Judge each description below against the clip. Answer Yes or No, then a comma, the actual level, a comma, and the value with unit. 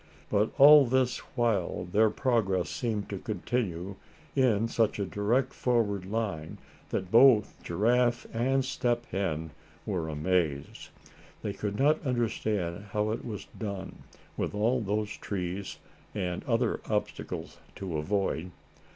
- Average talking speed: No, slow, 125 wpm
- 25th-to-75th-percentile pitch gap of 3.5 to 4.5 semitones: Yes, average, 4.1 semitones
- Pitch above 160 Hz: No, low, 105 Hz